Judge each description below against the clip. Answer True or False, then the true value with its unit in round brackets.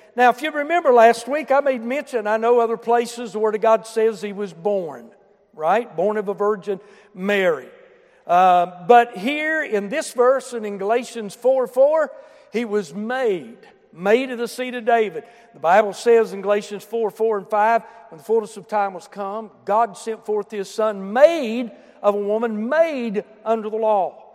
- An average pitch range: True (3.1 semitones)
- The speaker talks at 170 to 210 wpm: True (180 wpm)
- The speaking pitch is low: False (225 Hz)